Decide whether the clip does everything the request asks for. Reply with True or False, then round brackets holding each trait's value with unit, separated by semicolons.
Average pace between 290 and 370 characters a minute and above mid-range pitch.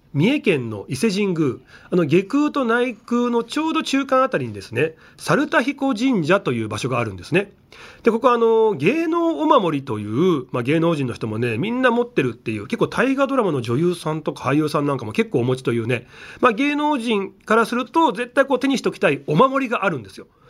False (420 characters per minute; 225 Hz)